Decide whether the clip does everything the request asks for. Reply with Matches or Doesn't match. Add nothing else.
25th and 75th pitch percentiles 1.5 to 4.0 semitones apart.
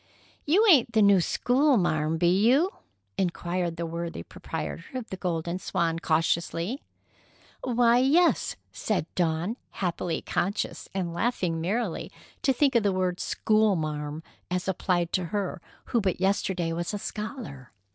Doesn't match